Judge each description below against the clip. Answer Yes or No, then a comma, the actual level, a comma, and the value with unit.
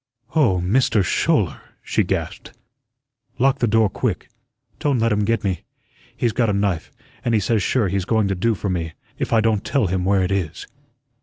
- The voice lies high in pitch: No, low, 105 Hz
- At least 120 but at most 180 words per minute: No, average, 190 wpm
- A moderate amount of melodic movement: Yes, average, 3.5 semitones